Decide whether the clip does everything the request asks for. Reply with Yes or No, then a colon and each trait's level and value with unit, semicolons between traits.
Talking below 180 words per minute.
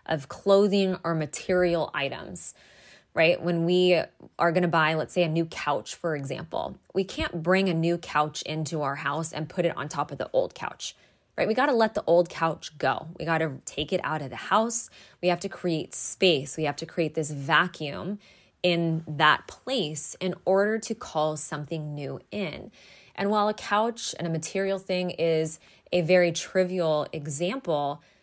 No: average, 185 wpm